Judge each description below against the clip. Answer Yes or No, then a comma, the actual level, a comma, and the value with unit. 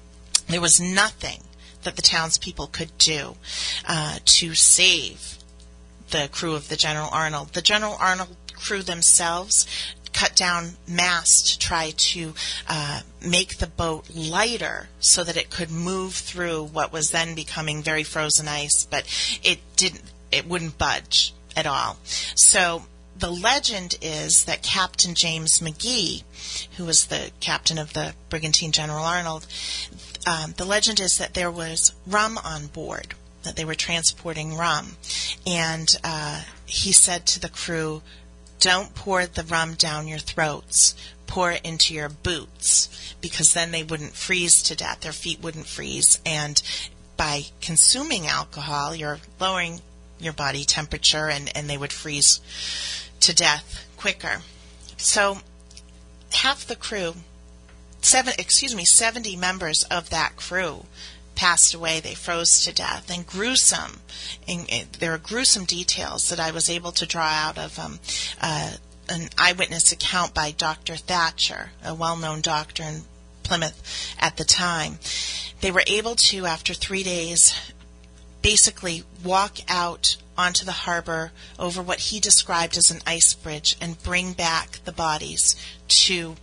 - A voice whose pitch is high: No, medium, 160 Hz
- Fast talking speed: No, average, 145 wpm